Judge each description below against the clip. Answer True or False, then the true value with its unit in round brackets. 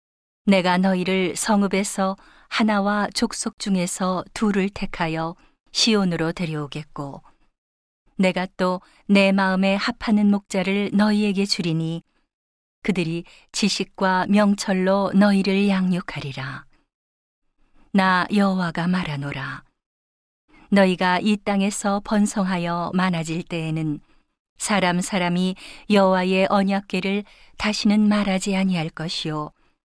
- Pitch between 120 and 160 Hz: False (190 Hz)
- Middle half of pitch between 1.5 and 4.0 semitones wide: True (2.7 semitones)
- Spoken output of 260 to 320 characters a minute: False (240 characters per minute)